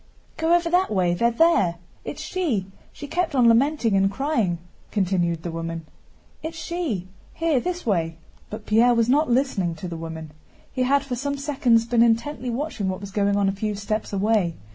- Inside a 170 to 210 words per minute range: Yes, average, 185 wpm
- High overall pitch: Yes, high, 230 Hz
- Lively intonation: Yes, wide, 6.8 semitones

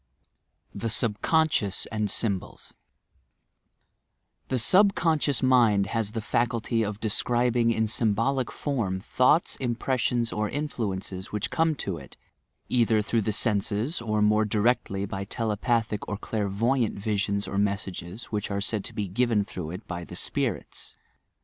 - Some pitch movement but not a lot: Yes, average, 3.2 semitones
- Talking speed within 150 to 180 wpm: No, average, 140 wpm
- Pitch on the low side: Yes, low, 110 Hz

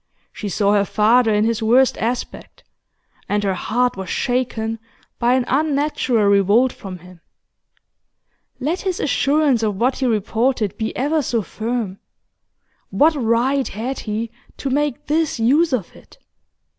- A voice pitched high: Yes, high, 235 Hz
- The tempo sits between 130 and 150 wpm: Yes, average, 145 wpm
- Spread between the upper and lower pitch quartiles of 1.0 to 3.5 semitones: No, average, 4.1 semitones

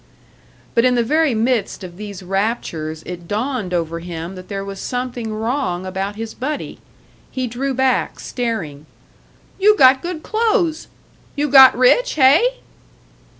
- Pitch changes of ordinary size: No, wide, 6.1 semitones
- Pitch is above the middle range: Yes, high, 235 Hz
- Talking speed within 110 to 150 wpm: Yes, average, 145 wpm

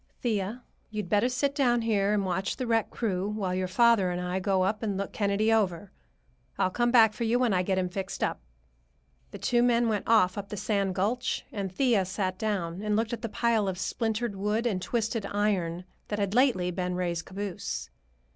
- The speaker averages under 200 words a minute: No, fast, 205 wpm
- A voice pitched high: Yes, high, 205 Hz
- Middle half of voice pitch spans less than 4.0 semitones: Yes, average, 3.4 semitones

